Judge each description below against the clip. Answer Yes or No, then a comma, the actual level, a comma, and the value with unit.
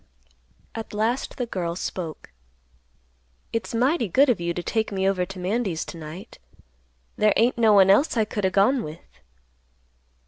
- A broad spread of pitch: No, average, 4.2 semitones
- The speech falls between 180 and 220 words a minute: No, average, 165 wpm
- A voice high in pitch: Yes, high, 205 Hz